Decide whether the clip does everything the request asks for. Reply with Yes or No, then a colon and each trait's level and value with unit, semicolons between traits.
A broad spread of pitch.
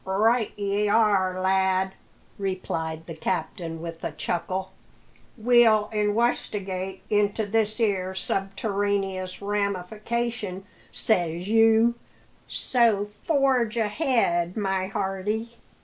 No: average, 2.9 semitones